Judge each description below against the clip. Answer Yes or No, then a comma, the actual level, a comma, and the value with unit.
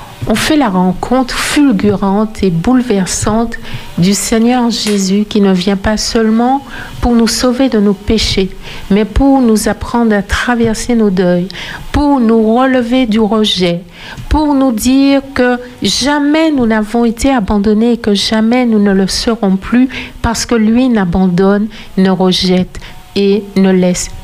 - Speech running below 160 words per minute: Yes, average, 150 wpm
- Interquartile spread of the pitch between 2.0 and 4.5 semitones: Yes, average, 3.9 semitones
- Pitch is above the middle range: Yes, high, 220 Hz